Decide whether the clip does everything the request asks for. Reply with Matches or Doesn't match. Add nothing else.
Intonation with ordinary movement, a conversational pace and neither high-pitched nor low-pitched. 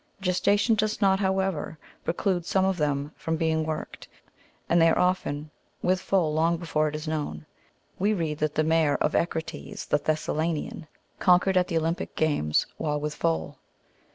Matches